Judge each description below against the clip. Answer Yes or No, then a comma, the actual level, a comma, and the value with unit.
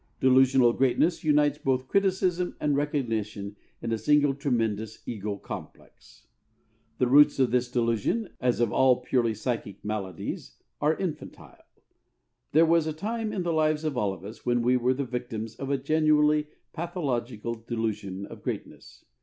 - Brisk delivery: No, average, 155 wpm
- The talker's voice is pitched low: Yes, low, 130 Hz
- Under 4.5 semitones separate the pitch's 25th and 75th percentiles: No, average, 4.9 semitones